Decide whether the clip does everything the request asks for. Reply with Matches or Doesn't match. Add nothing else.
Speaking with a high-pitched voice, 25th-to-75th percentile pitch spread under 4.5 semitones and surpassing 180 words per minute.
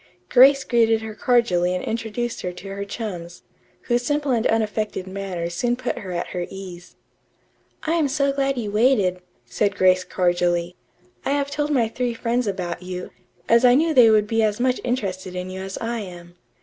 Doesn't match